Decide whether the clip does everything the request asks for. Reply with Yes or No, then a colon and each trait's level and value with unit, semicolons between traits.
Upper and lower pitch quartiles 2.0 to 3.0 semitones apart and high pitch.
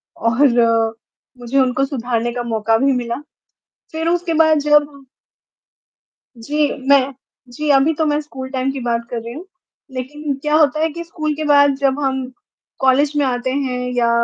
No: average, 3.4 semitones; very high, 270 Hz